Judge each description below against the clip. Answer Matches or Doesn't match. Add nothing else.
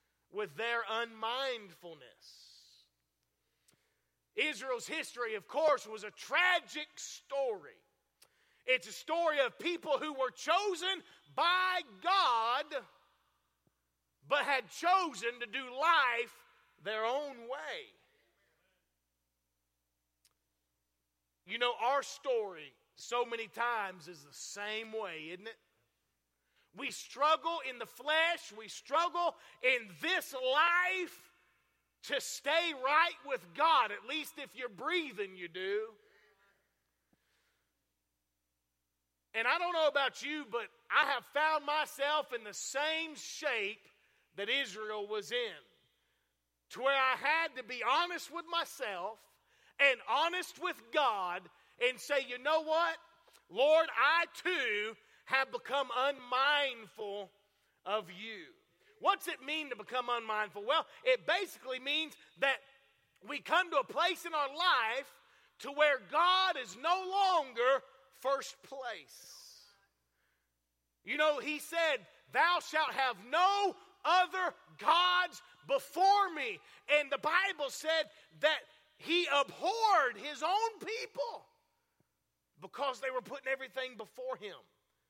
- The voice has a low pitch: Doesn't match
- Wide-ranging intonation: Matches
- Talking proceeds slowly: Matches